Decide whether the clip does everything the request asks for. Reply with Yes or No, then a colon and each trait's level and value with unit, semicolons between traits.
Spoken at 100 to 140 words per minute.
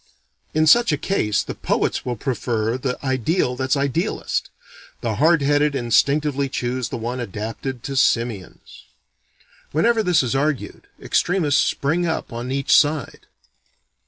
Yes: slow, 135 wpm